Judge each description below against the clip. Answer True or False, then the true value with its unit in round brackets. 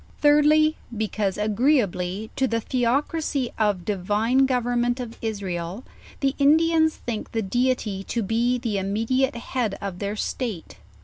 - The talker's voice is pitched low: False (230 Hz)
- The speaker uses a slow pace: True (130 wpm)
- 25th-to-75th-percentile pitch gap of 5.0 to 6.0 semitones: False (4.3 semitones)